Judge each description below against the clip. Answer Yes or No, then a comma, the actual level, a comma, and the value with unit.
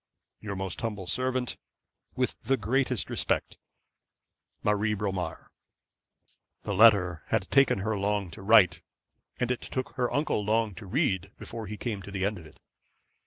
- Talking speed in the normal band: Yes, average, 155 wpm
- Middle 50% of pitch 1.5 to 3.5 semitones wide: Yes, average, 3.2 semitones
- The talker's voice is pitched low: Yes, low, 105 Hz